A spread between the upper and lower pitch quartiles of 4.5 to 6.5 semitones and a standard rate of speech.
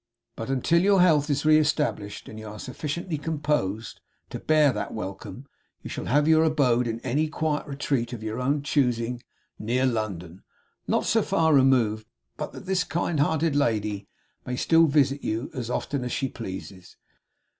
Yes: average, 5.2 semitones; average, 170 wpm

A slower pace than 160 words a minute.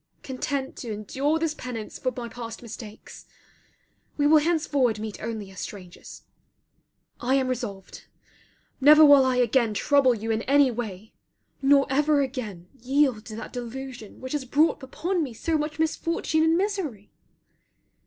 Yes: average, 150 wpm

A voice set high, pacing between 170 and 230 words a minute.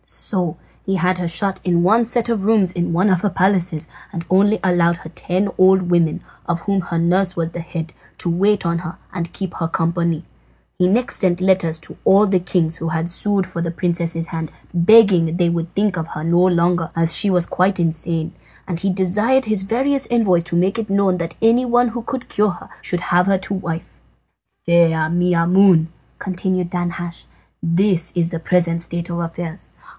No: medium, 180 Hz; average, 195 wpm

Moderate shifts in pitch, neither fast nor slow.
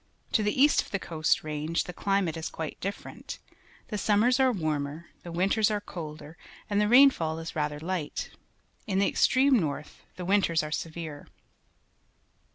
Yes: average, 4.8 semitones; average, 165 wpm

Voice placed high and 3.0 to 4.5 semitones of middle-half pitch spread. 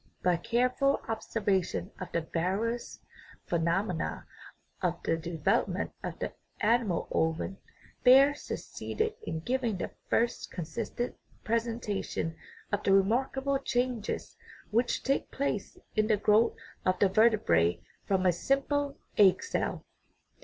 No: high, 215 Hz; average, 5.2 semitones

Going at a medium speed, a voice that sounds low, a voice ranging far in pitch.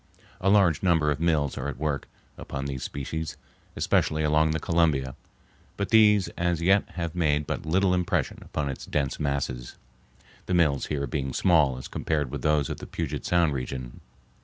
No: average, 175 wpm; very low, 75 Hz; average, 3.7 semitones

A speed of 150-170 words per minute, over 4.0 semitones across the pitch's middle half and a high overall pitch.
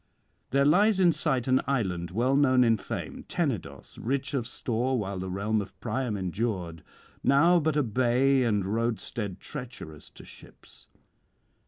No: average, 155 wpm; average, 5.0 semitones; low, 120 Hz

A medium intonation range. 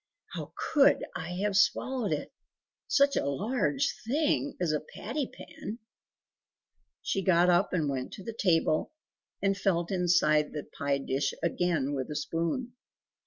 No: wide, 7.0 semitones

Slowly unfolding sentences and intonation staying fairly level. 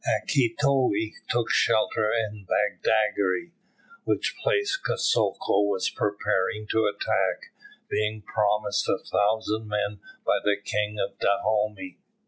Yes: slow, 110 wpm; narrow, 2.2 semitones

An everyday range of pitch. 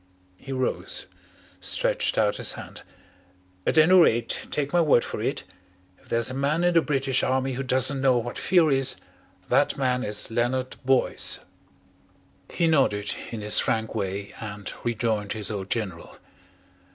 Yes: average, 3.8 semitones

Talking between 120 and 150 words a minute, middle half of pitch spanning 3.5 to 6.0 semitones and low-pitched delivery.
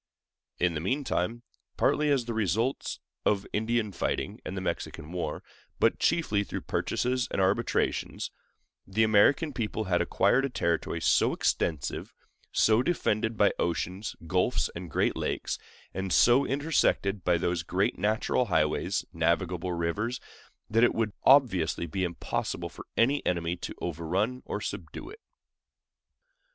Yes: average, 140 wpm; average, 5.2 semitones; low, 100 Hz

